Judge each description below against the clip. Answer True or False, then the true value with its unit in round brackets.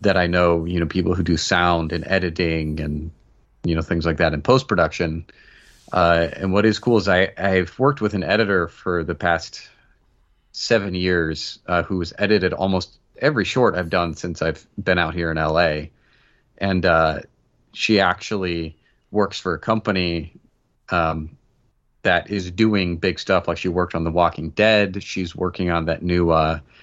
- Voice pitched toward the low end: True (85 Hz)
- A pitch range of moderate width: False (2.3 semitones)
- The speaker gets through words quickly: False (180 wpm)